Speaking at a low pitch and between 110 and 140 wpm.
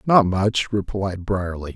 Yes: low, 100 Hz; slow, 135 wpm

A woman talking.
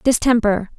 Yes: female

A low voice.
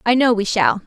No: high, 230 Hz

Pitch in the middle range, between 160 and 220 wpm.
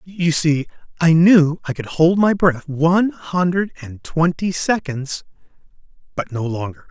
No: medium, 160 Hz; average, 150 wpm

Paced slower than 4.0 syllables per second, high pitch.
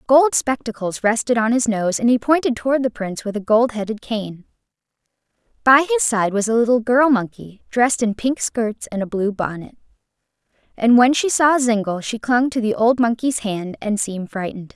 No: 5.3 syllables/s; high, 230 Hz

